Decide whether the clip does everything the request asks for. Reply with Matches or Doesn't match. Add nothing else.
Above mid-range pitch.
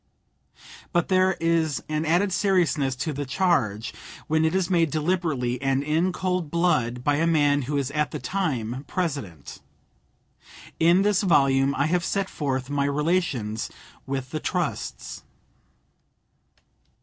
Doesn't match